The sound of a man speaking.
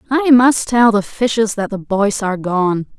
No: female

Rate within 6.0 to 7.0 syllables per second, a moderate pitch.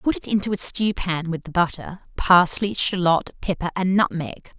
No: 4.6 syllables/s; medium, 180 Hz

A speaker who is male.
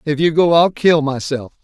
Yes: male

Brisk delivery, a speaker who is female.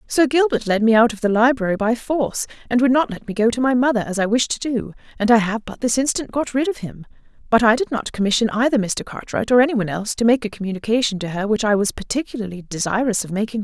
Yes: fast, 265 wpm; female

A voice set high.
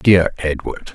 No: very low, 85 Hz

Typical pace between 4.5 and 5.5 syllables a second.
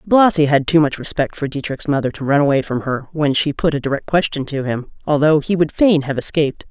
No: 5.8 syllables/s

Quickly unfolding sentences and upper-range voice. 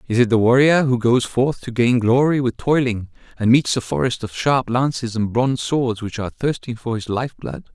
No: fast, 225 wpm; low, 120 Hz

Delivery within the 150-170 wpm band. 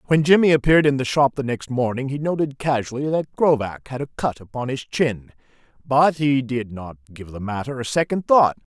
No: fast, 205 wpm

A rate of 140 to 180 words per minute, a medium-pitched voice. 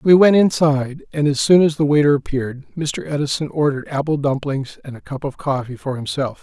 No: fast, 205 wpm; medium, 145 Hz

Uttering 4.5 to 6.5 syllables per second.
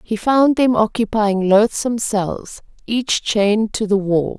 No: 3.9 syllables/s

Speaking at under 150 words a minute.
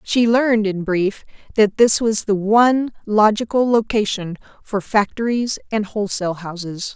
Yes: average, 140 wpm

